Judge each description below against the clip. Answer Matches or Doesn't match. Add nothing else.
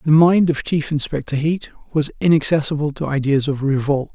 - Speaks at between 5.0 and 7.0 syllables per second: Matches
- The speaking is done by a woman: Doesn't match